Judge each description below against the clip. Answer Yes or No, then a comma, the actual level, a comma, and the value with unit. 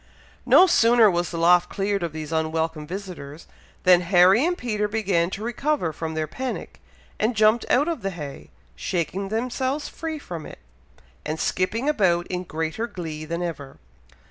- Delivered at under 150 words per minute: No, average, 165 wpm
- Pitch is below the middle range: No, medium, 185 Hz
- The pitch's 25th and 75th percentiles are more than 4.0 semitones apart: Yes, wide, 5.6 semitones